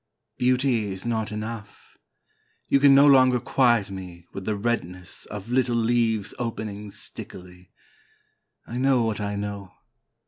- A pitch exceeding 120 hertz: No, low, 110 Hz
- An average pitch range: Yes, average, 3.4 semitones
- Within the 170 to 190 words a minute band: No, slow, 135 wpm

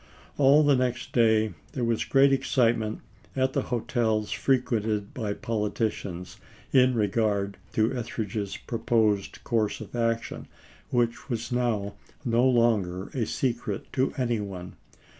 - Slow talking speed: Yes, slow, 130 wpm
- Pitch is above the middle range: No, low, 115 Hz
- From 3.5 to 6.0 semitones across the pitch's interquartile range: No, average, 2.8 semitones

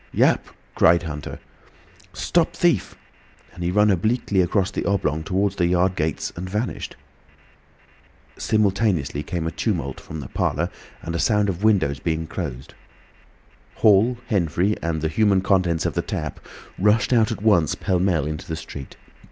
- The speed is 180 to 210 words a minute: No, average, 155 wpm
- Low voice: Yes, very low, 90 Hz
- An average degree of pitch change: Yes, average, 4.3 semitones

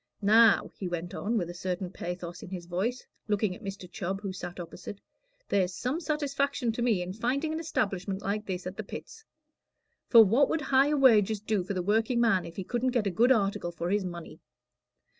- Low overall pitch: No, high, 205 Hz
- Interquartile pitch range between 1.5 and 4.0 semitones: No, average, 4.7 semitones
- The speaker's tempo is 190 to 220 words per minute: Yes, average, 200 wpm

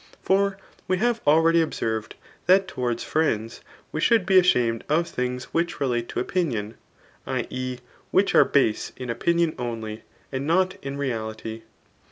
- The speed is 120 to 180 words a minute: Yes, average, 150 wpm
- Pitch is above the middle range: No, medium, 140 Hz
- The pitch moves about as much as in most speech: No, wide, 6.7 semitones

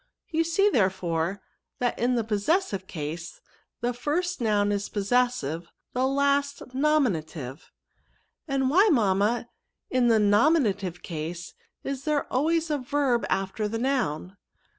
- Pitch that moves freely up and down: Yes, wide, 6.6 semitones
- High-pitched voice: Yes, high, 240 Hz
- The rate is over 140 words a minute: No, slow, 135 wpm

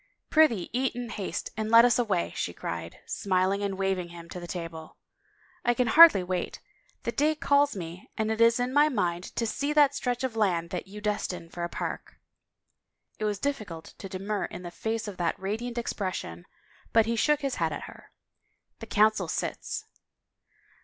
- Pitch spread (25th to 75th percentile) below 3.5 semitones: No, average, 5.2 semitones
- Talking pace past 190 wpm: Yes, average, 200 wpm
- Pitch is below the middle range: No, high, 210 Hz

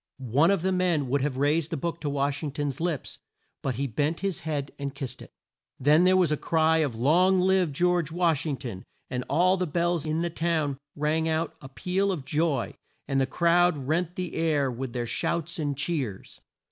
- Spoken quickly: Yes, fast, 210 wpm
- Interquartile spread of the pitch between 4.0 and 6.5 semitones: No, average, 3.6 semitones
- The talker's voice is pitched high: No, medium, 155 Hz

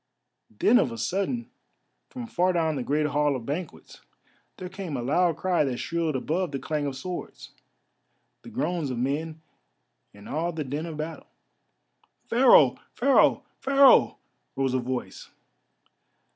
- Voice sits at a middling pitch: Yes, medium, 155 Hz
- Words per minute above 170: No, average, 145 wpm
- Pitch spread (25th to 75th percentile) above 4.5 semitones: Yes, average, 4.9 semitones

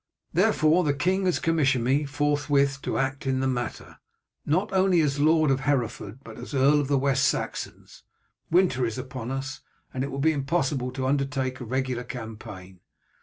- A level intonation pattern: Yes, narrow, 2.3 semitones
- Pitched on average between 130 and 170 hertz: Yes, low, 135 Hz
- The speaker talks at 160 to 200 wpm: Yes, average, 175 wpm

